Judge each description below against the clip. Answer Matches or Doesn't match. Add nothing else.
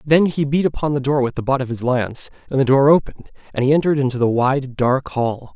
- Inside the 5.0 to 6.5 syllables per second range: Matches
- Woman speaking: Doesn't match